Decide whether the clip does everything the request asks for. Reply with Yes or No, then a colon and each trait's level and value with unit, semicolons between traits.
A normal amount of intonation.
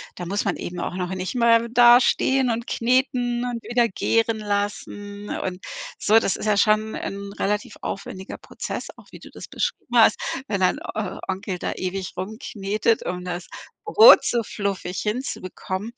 Yes: average, 3.6 semitones